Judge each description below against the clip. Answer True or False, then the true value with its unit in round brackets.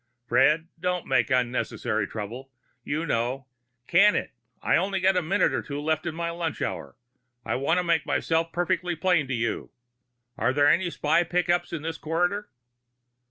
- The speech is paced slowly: False (175 wpm)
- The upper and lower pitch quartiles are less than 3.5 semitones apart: False (4.7 semitones)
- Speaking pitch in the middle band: True (160 Hz)